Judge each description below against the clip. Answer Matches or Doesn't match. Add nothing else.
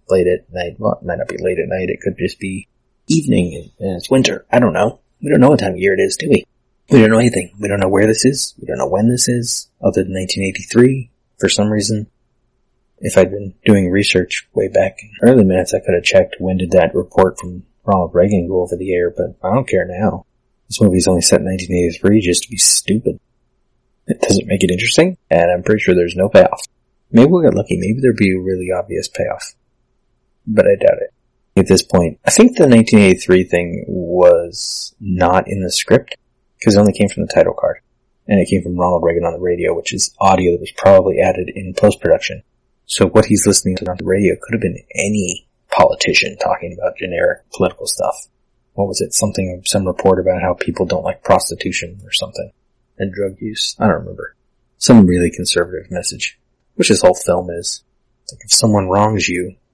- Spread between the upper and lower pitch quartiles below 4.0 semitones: Matches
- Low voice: Matches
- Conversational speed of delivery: Doesn't match